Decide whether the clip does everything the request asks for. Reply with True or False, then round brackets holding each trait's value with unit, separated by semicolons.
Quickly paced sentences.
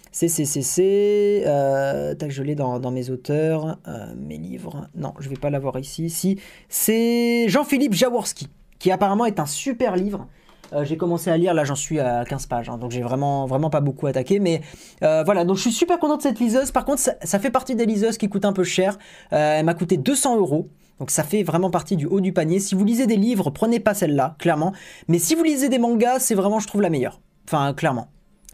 True (225 wpm)